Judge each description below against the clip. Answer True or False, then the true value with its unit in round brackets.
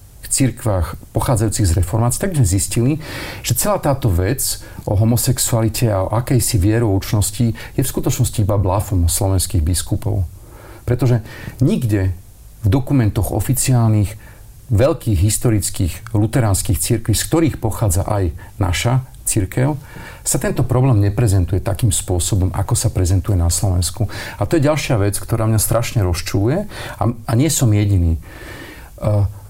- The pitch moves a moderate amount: True (3.3 semitones)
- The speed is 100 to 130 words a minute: True (125 wpm)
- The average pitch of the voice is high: False (110 Hz)